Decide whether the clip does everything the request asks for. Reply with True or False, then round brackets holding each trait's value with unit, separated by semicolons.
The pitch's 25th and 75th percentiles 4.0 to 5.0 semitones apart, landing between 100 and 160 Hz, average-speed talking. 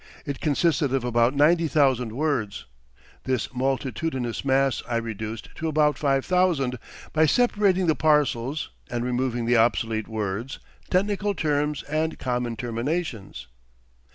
False (4.7 semitones; 135 Hz; 125 wpm)